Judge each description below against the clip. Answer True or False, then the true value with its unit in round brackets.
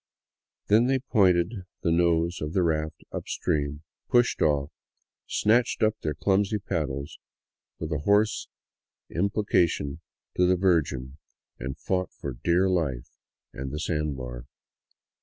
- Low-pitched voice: True (85 Hz)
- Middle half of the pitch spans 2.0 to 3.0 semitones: False (4.8 semitones)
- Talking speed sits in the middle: False (130 wpm)